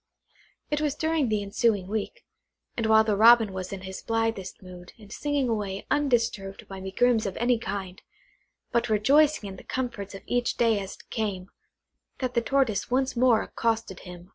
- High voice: Yes, high, 220 Hz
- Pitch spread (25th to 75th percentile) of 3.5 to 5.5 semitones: Yes, average, 3.9 semitones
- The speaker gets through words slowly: No, average, 175 wpm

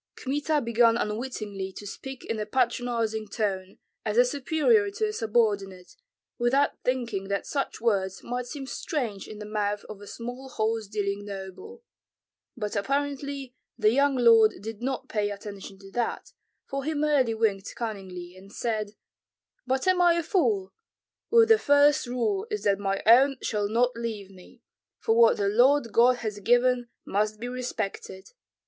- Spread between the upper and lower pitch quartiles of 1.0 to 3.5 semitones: No, average, 4.6 semitones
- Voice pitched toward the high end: Yes, high, 230 Hz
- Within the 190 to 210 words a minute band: No, average, 165 wpm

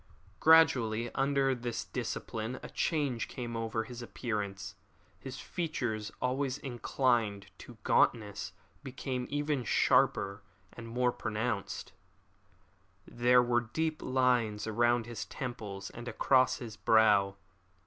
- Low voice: Yes, low, 120 Hz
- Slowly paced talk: Yes, slow, 110 wpm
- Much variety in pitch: No, average, 2.8 semitones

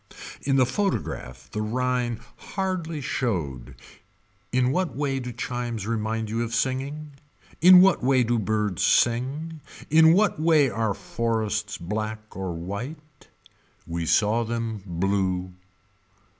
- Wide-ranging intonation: No, average, 4.8 semitones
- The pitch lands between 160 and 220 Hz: No, low, 115 Hz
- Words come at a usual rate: No, slow, 125 wpm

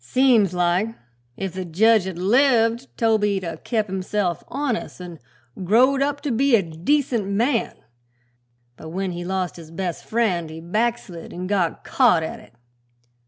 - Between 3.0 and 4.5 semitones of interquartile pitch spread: No, average, 5.0 semitones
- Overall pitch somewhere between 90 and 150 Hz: No, high, 200 Hz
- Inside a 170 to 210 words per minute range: No, average, 155 wpm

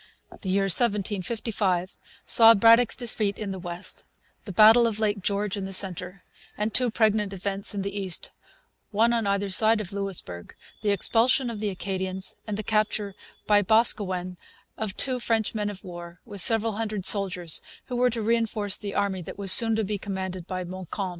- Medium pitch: No, high, 205 Hz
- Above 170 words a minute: Yes, average, 180 wpm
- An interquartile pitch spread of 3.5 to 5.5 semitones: No, narrow, 2.6 semitones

